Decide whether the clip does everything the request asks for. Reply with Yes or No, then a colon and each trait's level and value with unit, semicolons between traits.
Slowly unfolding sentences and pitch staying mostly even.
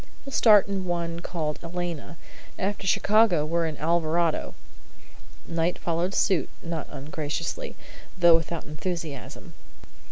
Yes: slow, 115 wpm; narrow, 2.3 semitones